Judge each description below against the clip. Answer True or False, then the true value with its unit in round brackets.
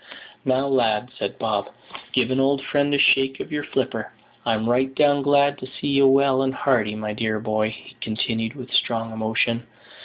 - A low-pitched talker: True (130 Hz)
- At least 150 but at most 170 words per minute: False (185 wpm)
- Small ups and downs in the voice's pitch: False (3.6 semitones)